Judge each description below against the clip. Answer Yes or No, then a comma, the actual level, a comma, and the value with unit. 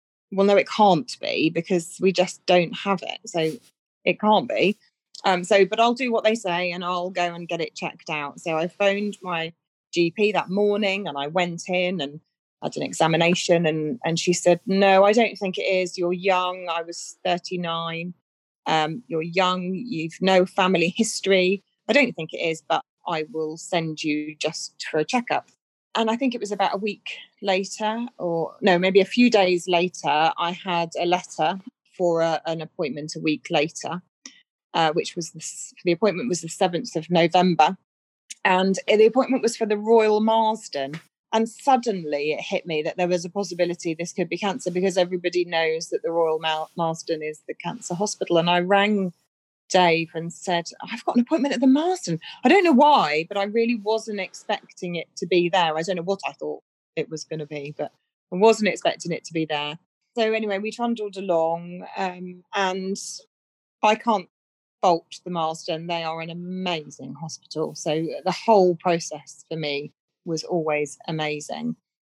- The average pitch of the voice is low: No, medium, 180 Hz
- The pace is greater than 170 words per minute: Yes, average, 185 wpm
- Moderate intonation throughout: Yes, average, 3.6 semitones